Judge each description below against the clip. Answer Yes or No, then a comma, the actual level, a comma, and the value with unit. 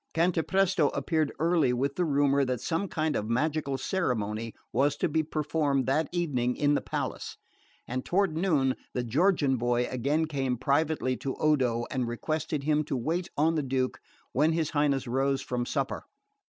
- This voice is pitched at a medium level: Yes, medium, 145 Hz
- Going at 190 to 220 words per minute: No, average, 165 wpm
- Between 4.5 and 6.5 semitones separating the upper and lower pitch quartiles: No, average, 3.7 semitones